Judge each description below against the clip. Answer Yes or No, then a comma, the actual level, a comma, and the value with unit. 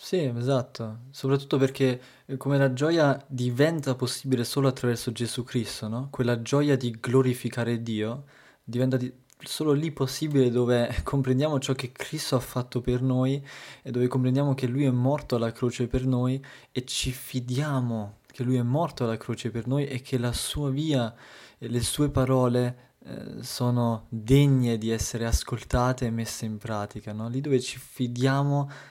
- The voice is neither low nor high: No, low, 130 Hz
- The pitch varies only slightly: Yes, narrow, 2.1 semitones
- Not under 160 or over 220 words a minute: Yes, average, 165 wpm